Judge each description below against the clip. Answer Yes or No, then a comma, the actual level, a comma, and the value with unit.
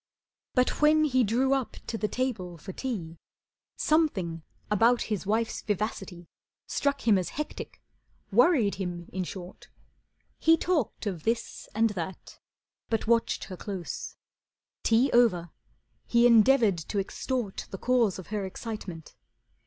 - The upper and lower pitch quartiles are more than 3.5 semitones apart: Yes, average, 5.0 semitones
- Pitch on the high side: Yes, high, 220 Hz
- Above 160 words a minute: No, slow, 135 wpm